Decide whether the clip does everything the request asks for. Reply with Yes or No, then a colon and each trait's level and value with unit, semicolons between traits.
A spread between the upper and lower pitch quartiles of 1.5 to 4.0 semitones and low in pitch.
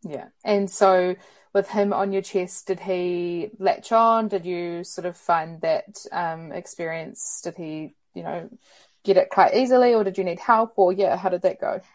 No: narrow, 2.6 semitones; high, 190 Hz